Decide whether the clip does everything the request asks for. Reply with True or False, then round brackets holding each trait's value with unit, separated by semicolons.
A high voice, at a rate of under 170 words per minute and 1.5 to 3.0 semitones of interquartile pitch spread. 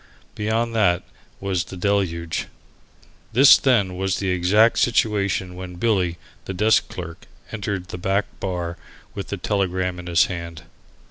False (95 Hz; 140 wpm; 2.6 semitones)